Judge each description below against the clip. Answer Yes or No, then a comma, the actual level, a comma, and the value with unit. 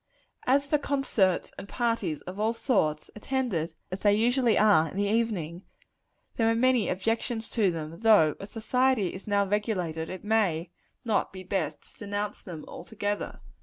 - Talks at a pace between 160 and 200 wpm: Yes, average, 165 wpm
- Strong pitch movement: No, average, 3.9 semitones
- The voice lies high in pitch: Yes, high, 205 Hz